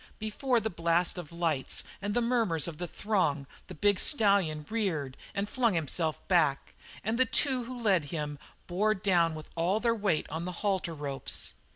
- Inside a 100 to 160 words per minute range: No, average, 180 wpm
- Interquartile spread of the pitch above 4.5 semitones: Yes, average, 5.1 semitones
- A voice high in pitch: No, medium, 180 Hz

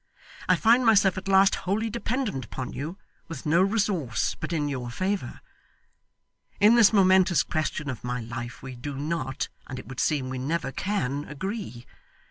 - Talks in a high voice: No, medium, 160 Hz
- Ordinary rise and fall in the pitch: No, wide, 7.1 semitones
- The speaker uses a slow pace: No, average, 165 wpm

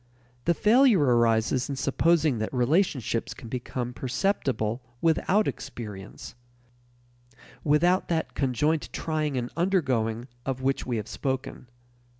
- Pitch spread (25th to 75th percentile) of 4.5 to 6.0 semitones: Yes, average, 5.2 semitones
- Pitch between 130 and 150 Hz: Yes, low, 135 Hz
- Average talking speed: No, slow, 115 wpm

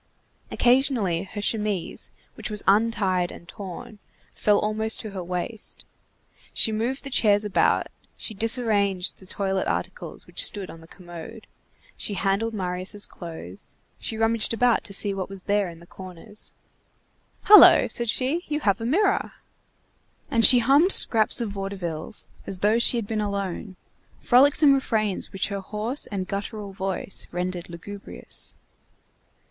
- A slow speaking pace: No, average, 145 wpm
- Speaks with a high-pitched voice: Yes, high, 205 Hz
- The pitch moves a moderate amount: Yes, average, 3.2 semitones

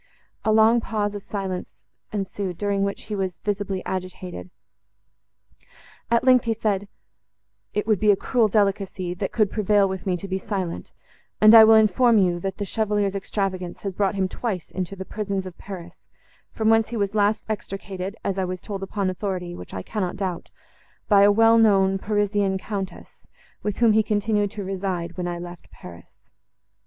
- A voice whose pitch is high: Yes, high, 200 Hz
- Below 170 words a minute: No, average, 175 wpm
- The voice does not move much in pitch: Yes, narrow, 2.1 semitones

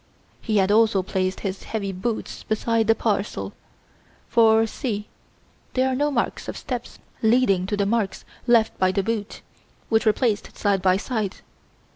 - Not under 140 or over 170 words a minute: Yes, average, 160 wpm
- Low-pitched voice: No, high, 215 Hz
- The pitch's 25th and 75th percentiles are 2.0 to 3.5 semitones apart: Yes, average, 2.7 semitones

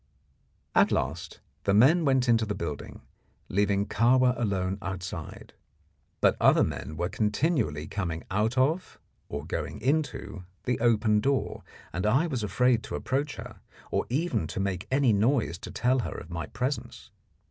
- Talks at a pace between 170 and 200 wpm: No, average, 155 wpm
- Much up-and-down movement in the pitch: Yes, wide, 5.8 semitones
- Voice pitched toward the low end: Yes, low, 110 Hz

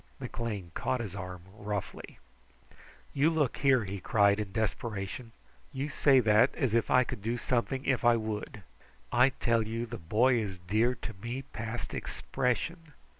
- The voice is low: Yes, low, 115 Hz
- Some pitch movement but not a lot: Yes, average, 3.5 semitones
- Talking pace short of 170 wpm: Yes, average, 160 wpm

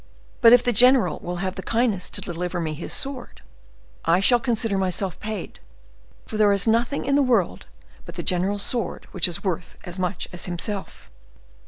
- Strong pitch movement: No, average, 4.6 semitones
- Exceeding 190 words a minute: No, average, 185 wpm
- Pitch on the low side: No, high, 200 Hz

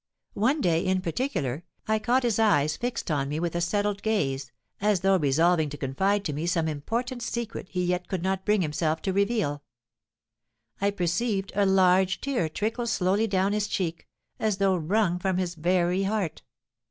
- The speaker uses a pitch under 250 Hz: Yes, high, 190 Hz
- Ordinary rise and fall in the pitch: Yes, average, 3.9 semitones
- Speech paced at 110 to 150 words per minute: No, average, 175 wpm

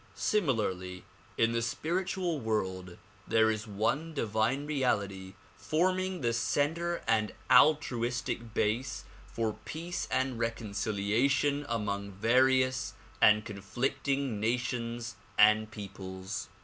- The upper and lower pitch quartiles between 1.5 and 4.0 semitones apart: No, average, 4.7 semitones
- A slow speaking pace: Yes, slow, 95 wpm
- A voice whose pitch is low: Yes, low, 115 Hz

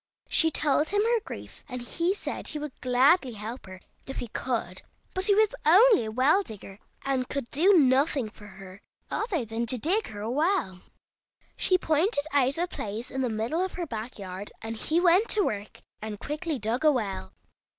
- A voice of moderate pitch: No, very high, 265 Hz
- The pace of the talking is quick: No, average, 195 wpm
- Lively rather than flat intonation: Yes, wide, 7.8 semitones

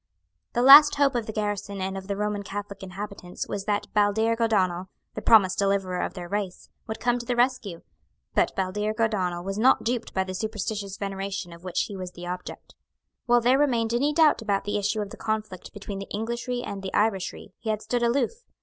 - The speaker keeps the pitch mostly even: No, average, 3.1 semitones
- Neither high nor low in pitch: No, high, 205 Hz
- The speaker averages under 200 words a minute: No, fast, 205 wpm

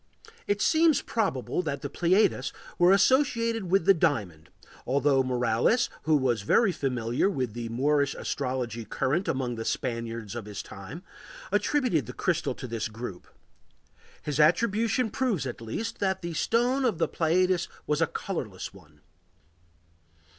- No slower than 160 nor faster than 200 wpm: No, average, 145 wpm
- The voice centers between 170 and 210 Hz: No, medium, 145 Hz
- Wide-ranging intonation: Yes, wide, 8.8 semitones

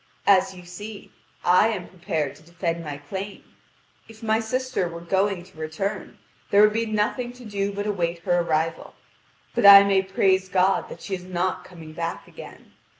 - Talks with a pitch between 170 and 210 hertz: Yes, high, 190 Hz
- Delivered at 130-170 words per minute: No, average, 180 wpm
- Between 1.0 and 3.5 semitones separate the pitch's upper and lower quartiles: Yes, average, 3.1 semitones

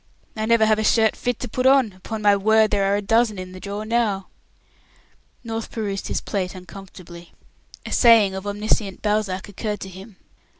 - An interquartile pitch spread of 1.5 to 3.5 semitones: Yes, narrow, 2.4 semitones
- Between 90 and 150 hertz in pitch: No, high, 210 Hz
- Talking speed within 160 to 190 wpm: Yes, average, 185 wpm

